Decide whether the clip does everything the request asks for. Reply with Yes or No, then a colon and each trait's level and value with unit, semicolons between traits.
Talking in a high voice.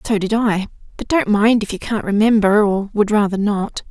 Yes: high, 210 Hz